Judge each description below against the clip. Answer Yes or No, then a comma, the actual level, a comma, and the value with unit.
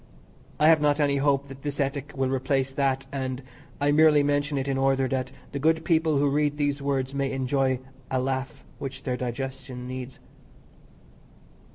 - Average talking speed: Yes, average, 175 wpm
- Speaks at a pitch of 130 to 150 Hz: Yes, low, 135 Hz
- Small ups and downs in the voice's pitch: Yes, narrow, 1.5 semitones